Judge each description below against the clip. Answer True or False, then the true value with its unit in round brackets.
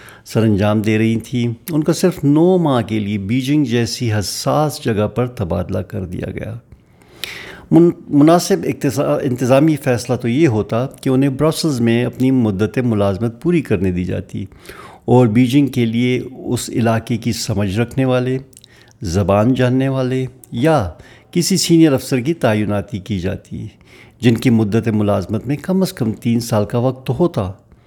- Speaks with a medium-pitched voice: False (120 Hz)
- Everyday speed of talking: True (155 wpm)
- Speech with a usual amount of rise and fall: True (3.9 semitones)